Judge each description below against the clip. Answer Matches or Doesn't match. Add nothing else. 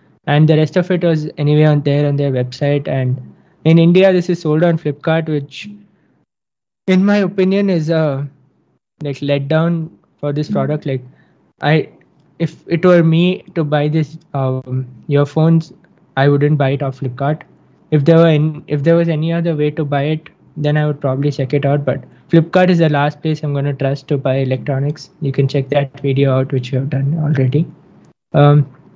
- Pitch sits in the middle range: Matches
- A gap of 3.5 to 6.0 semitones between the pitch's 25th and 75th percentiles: Doesn't match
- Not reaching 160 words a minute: Doesn't match